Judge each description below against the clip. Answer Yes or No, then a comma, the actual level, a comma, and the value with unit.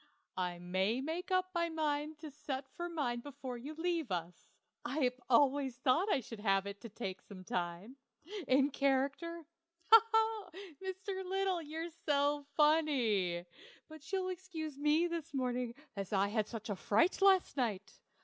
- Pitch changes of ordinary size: No, wide, 6.4 semitones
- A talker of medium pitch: No, very high, 280 Hz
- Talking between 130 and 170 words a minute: Yes, average, 155 wpm